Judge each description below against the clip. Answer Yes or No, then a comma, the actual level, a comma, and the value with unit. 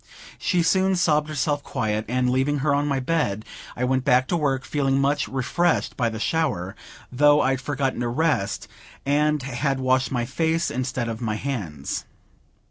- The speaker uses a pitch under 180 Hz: Yes, low, 135 Hz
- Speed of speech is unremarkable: Yes, average, 170 wpm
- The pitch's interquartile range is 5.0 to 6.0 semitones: No, average, 3.3 semitones